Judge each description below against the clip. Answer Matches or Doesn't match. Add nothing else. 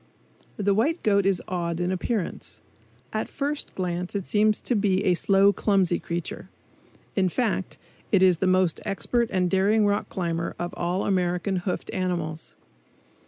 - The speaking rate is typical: Matches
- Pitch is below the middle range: Doesn't match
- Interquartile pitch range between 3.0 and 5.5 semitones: Doesn't match